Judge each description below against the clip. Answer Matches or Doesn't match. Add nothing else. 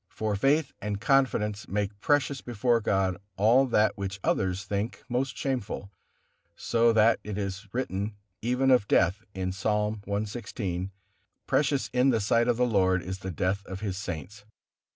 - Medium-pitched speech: Doesn't match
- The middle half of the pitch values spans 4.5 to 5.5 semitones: Doesn't match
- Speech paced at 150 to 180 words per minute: Matches